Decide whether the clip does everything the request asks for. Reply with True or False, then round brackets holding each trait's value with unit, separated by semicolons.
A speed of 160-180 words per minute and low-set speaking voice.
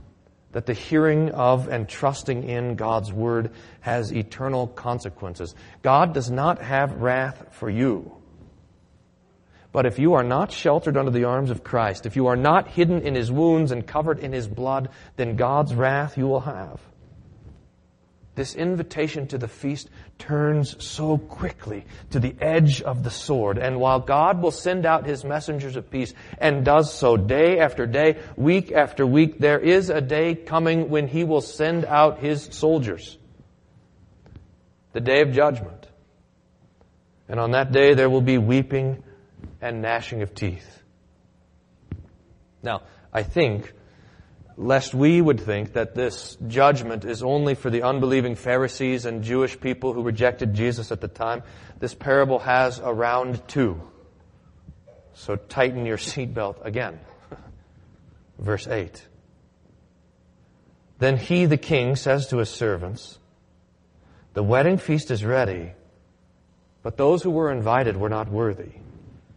False (145 wpm; 125 Hz)